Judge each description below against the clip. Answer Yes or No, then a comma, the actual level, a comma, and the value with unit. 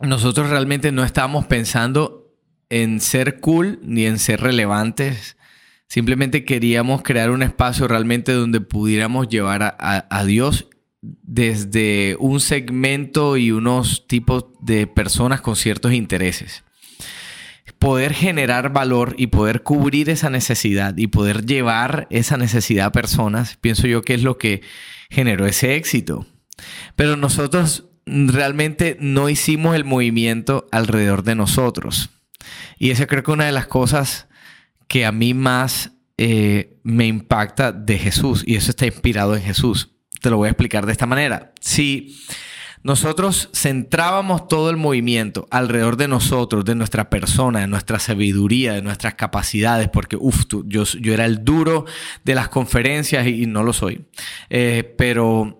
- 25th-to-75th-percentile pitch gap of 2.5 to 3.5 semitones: No, average, 3.9 semitones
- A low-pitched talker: Yes, low, 120 Hz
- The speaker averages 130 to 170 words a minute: Yes, average, 150 wpm